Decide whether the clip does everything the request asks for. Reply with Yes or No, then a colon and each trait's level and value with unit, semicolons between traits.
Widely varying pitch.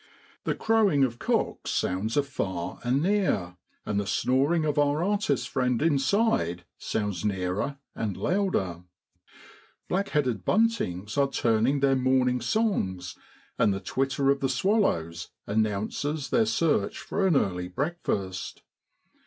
Yes: wide, 8.1 semitones